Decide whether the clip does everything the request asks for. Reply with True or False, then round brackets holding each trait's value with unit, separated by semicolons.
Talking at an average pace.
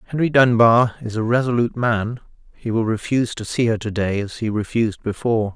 True (195 wpm)